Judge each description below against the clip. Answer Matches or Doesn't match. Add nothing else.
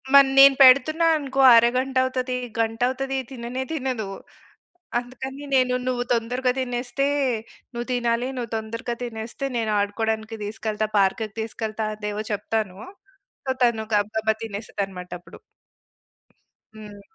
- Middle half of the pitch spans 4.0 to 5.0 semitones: Doesn't match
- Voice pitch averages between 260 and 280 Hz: Doesn't match